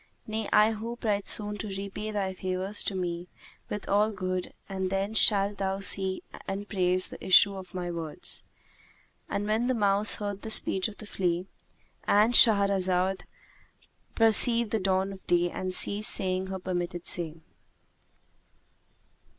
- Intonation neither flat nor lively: No, narrow, 2.1 semitones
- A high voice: Yes, high, 195 Hz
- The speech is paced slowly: No, average, 150 wpm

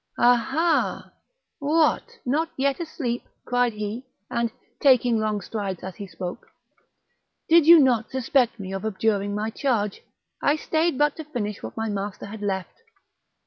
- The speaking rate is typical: Yes, average, 150 wpm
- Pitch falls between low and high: No, high, 235 Hz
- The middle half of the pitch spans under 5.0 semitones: No, wide, 5.5 semitones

